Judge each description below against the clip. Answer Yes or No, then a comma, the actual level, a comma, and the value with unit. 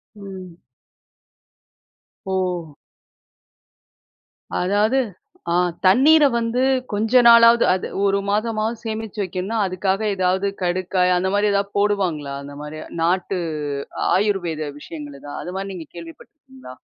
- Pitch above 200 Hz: No, high, 195 Hz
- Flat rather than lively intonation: No, average, 3.2 semitones